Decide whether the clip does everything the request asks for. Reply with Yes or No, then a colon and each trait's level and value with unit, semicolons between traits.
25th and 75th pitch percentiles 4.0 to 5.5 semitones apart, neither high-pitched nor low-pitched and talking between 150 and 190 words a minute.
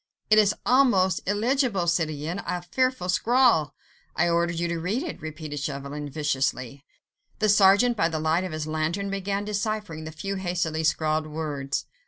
Yes: average, 4.6 semitones; medium, 170 Hz; average, 165 wpm